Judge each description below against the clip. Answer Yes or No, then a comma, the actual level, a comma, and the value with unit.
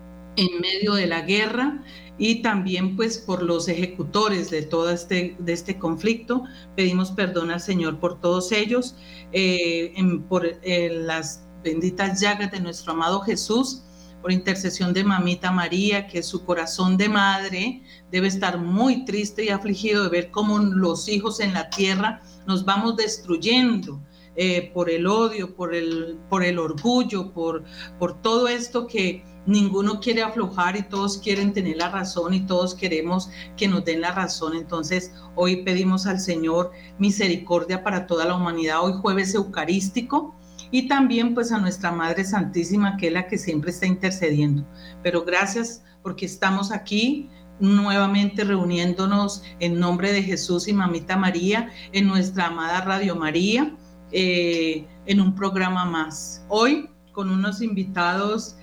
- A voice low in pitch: No, medium, 185 Hz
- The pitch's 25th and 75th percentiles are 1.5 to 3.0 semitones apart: Yes, narrow, 2.6 semitones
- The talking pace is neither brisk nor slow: Yes, average, 150 wpm